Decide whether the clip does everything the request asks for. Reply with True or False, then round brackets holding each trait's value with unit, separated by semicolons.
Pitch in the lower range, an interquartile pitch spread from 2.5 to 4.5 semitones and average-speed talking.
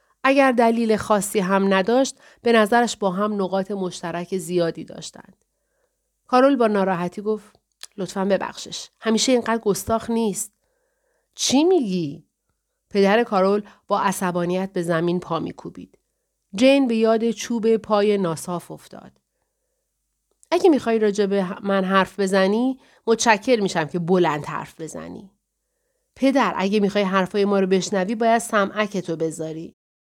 False (210 Hz; 4.1 semitones; 125 wpm)